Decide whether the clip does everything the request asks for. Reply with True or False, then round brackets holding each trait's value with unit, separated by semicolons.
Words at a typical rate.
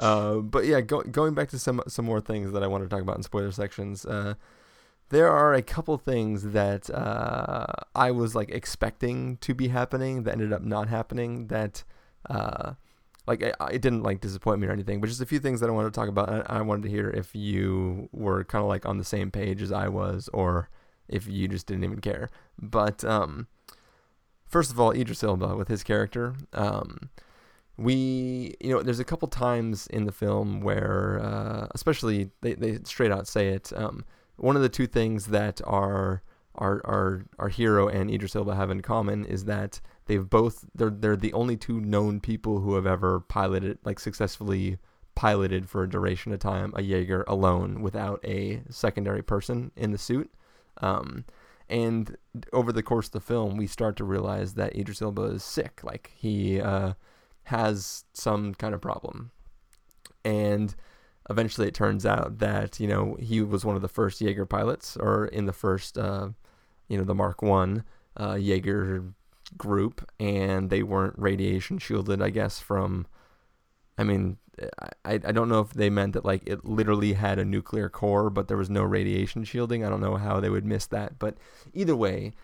True (195 wpm)